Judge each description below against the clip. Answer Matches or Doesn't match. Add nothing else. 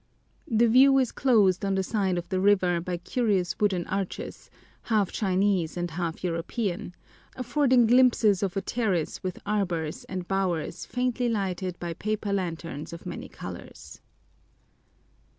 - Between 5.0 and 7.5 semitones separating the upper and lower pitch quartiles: Doesn't match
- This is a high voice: Matches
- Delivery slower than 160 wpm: Matches